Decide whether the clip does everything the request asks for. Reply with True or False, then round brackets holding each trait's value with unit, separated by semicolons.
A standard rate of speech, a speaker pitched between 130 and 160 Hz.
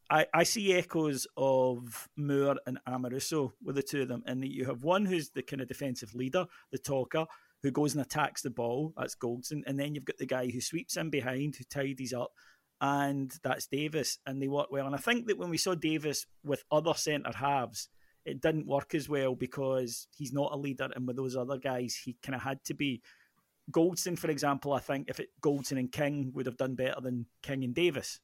False (220 wpm; 140 Hz)